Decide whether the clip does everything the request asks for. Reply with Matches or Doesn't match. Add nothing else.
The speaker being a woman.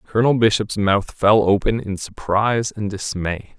Doesn't match